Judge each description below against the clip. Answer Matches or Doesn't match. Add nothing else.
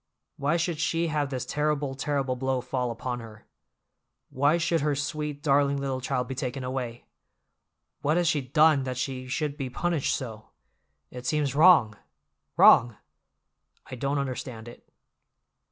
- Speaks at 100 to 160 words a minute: Matches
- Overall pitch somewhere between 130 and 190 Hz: Matches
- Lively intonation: Doesn't match